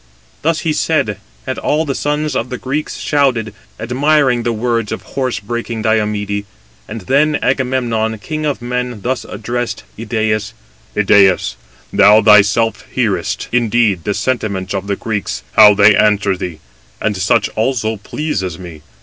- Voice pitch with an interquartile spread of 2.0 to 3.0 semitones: No, average, 3.9 semitones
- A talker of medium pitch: No, low, 115 Hz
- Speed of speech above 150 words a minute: No, average, 145 wpm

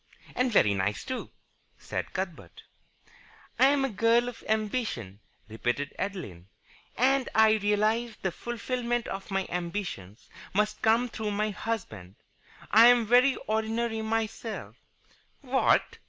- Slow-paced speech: Yes, slow, 130 wpm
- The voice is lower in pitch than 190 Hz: No, high, 220 Hz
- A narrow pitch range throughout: No, average, 3.8 semitones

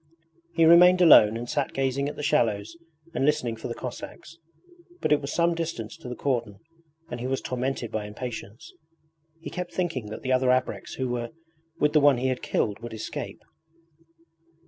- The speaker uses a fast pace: No, average, 185 wpm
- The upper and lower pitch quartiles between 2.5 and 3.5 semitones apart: No, average, 4.2 semitones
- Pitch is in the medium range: No, low, 130 Hz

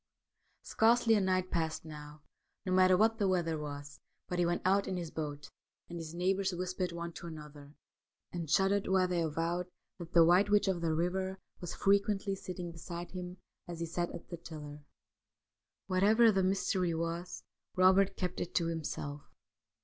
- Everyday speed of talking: Yes, average, 180 wpm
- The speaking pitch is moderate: Yes, medium, 175 Hz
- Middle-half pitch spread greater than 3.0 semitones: No, narrow, 2.4 semitones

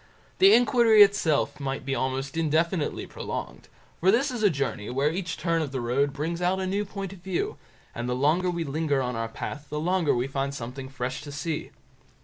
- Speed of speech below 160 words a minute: No, fast, 205 wpm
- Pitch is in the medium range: Yes, medium, 155 Hz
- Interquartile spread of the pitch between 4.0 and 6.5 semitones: Yes, average, 5.3 semitones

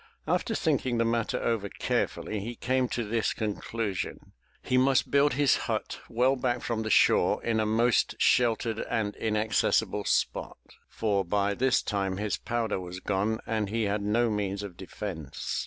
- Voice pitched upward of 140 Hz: No, low, 110 Hz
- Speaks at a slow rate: No, average, 170 wpm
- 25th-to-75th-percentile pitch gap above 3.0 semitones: No, narrow, 2.6 semitones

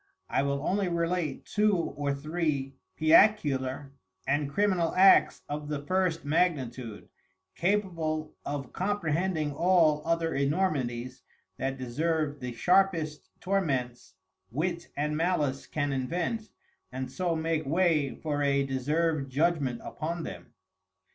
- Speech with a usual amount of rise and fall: Yes, average, 3.8 semitones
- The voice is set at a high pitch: No, medium, 155 Hz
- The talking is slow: Yes, slow, 115 wpm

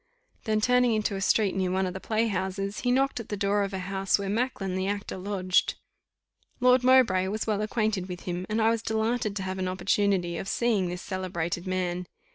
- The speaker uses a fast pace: Yes, fast, 215 wpm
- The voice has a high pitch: Yes, high, 195 Hz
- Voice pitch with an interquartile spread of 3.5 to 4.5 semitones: No, average, 2.8 semitones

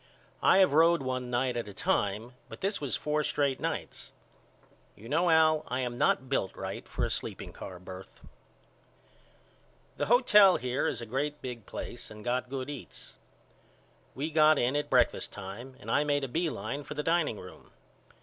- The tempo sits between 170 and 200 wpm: Yes, average, 180 wpm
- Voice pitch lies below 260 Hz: Yes, low, 135 Hz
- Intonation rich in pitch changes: No, average, 4.0 semitones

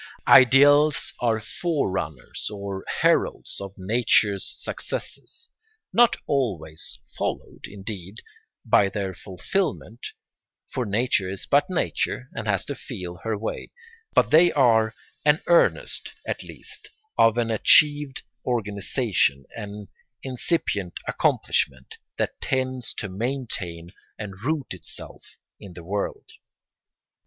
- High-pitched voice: No, low, 110 Hz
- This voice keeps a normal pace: No, slow, 110 wpm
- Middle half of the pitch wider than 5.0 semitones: Yes, wide, 5.4 semitones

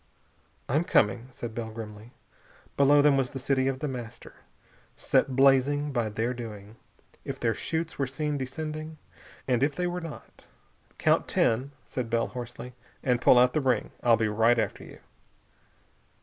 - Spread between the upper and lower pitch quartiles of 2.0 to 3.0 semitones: No, average, 3.6 semitones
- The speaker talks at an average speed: Yes, average, 165 wpm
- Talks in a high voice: No, low, 130 Hz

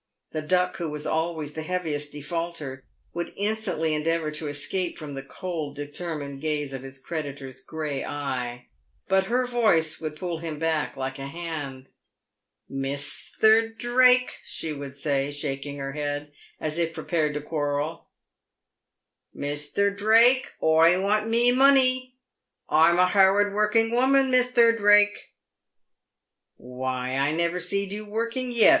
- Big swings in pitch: Yes, wide, 6.2 semitones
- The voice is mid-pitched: Yes, medium, 160 Hz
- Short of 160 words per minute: Yes, average, 145 wpm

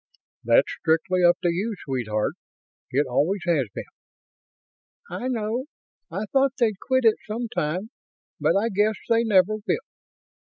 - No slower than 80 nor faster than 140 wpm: Yes, slow, 135 wpm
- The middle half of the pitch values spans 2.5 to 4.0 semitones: No, average, 5.2 semitones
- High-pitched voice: Yes, high, 205 Hz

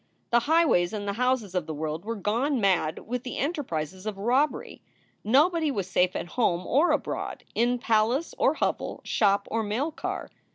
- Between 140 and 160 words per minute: No, average, 175 wpm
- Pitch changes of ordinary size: No, wide, 5.8 semitones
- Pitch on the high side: Yes, high, 225 Hz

